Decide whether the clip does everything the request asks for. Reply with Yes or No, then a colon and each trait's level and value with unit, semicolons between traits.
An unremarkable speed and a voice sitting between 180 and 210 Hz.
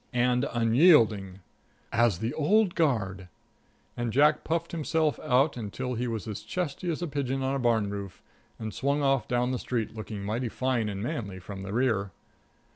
No: average, 175 wpm; low, 120 Hz